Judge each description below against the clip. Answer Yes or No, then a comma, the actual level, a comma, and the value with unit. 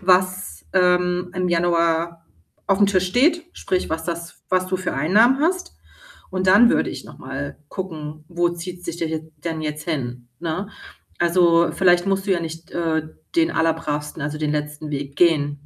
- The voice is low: No, medium, 170 Hz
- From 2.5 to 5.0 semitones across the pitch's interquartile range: Yes, average, 2.8 semitones